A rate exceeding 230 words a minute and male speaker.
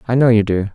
Yes: fast, 325 wpm; male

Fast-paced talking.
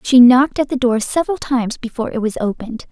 Yes: fast, 225 wpm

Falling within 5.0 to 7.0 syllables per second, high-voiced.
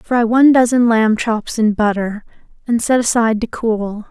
No: 4.7 syllables/s; high, 225 Hz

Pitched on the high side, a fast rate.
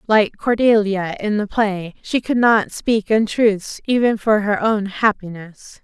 No: high, 210 Hz; average, 155 wpm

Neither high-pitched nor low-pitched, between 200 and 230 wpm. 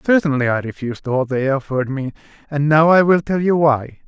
Yes: medium, 145 Hz; fast, 205 wpm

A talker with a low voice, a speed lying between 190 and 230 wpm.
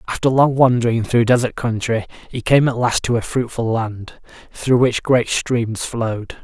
No: low, 120 Hz; average, 175 wpm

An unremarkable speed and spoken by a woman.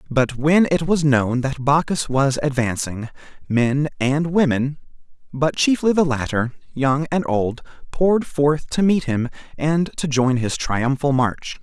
No: average, 155 wpm; male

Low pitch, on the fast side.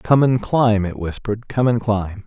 Yes: low, 110 Hz; fast, 210 wpm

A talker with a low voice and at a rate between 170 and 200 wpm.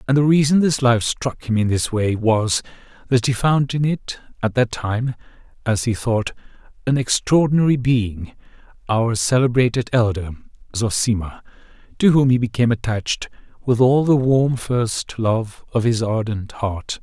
No: low, 120 Hz; average, 155 wpm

